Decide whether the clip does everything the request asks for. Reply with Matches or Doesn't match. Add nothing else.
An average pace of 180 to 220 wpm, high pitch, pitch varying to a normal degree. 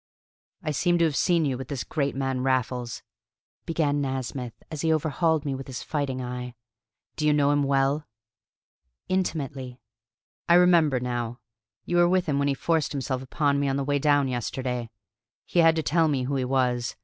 Doesn't match